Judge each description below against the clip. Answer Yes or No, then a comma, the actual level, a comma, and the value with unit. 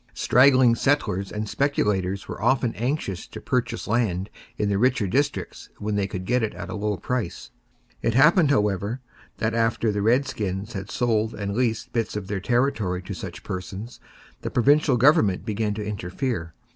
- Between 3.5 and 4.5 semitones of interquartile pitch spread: Yes, average, 3.9 semitones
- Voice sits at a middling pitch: No, low, 110 Hz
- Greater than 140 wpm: Yes, average, 170 wpm